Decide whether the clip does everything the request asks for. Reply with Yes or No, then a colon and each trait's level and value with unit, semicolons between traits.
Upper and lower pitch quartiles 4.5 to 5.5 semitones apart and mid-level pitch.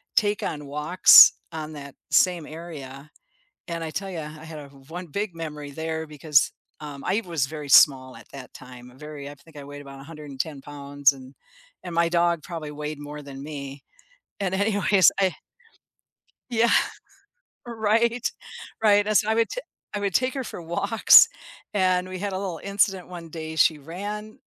Yes: average, 5.0 semitones; medium, 160 Hz